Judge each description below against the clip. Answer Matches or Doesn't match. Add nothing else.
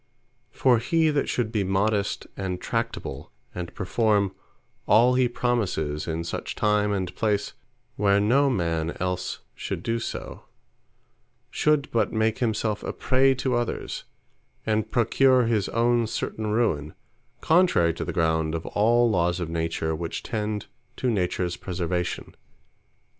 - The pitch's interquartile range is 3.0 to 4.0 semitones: Doesn't match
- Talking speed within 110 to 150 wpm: Matches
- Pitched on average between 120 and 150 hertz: Doesn't match